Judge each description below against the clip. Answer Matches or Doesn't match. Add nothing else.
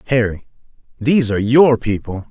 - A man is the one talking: Matches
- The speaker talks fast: Doesn't match